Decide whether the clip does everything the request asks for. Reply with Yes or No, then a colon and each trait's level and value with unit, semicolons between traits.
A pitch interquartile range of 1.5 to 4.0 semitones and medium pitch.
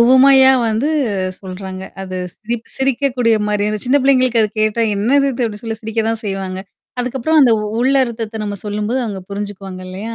No: average, 3.7 semitones; high, 225 Hz